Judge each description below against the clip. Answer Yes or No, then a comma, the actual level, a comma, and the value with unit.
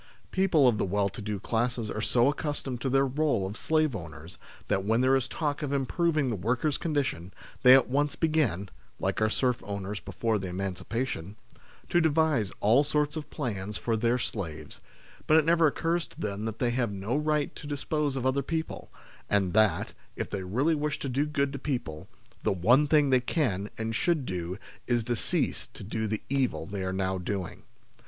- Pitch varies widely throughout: Yes, wide, 6.3 semitones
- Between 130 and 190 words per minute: No, average, 200 wpm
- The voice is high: No, low, 125 Hz